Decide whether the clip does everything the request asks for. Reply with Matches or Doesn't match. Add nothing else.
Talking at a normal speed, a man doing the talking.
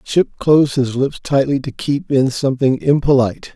Matches